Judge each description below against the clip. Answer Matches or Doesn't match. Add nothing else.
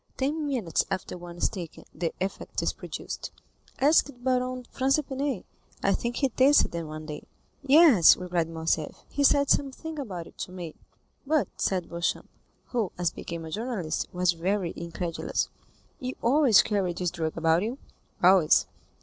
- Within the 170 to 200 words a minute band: Doesn't match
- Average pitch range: Doesn't match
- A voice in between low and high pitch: Doesn't match